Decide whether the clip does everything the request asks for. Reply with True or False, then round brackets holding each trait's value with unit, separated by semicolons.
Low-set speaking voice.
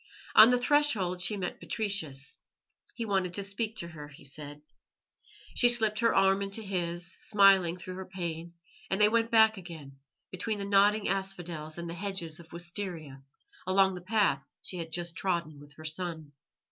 False (185 Hz)